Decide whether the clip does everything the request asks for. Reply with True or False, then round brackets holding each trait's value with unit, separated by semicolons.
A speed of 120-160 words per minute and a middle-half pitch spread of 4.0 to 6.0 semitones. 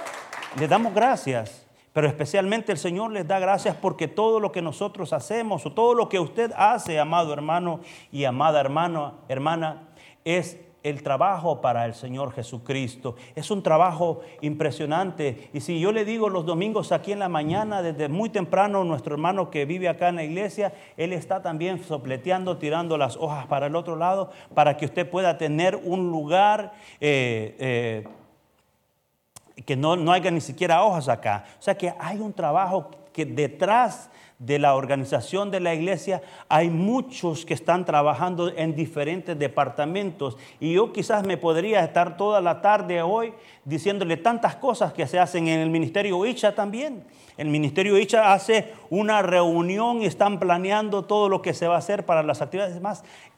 False (170 wpm; 4.7 semitones)